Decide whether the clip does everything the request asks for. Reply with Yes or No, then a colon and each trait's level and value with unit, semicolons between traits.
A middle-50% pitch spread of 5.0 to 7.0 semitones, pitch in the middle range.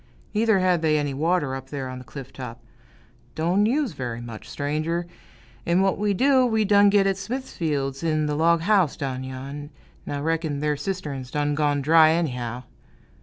Yes: wide, 5.4 semitones; medium, 155 Hz